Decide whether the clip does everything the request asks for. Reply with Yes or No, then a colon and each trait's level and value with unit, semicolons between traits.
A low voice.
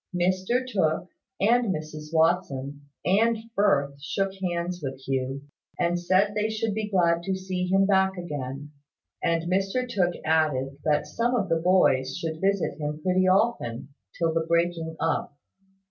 No: medium, 175 Hz